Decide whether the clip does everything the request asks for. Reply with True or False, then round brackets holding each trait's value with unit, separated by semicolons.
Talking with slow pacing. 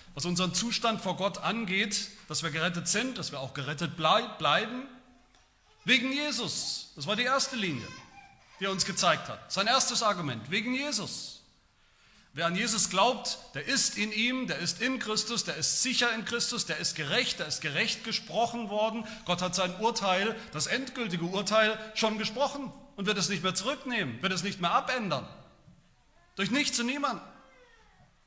False (175 wpm)